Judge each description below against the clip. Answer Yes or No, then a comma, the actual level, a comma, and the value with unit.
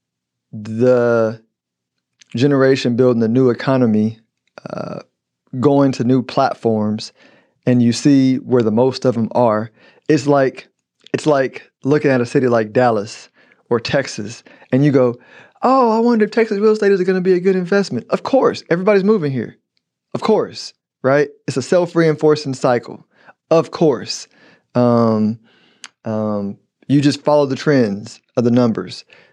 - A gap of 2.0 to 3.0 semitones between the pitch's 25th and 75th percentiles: No, average, 4.4 semitones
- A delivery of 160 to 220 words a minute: No, average, 150 wpm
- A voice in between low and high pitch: No, low, 130 Hz